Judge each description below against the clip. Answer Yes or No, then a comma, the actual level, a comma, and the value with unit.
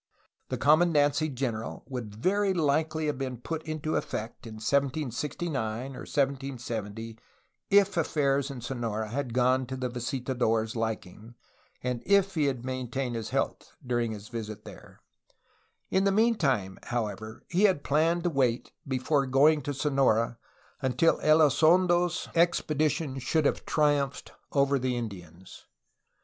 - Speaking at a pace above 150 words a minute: No, slow, 135 wpm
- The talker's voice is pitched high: No, low, 135 Hz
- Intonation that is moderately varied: Yes, average, 4.7 semitones